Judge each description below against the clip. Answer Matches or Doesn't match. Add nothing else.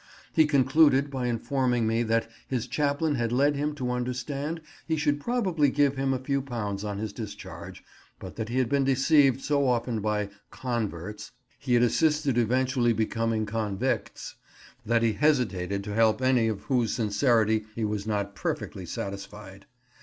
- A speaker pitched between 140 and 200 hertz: Doesn't match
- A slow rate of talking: Doesn't match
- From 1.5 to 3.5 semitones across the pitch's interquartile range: Doesn't match